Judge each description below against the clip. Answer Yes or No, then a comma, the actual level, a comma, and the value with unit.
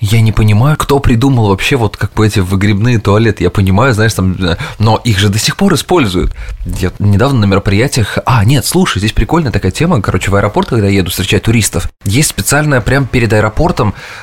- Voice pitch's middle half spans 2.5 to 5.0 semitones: Yes, average, 4.6 semitones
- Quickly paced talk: Yes, fast, 200 wpm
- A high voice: No, low, 110 Hz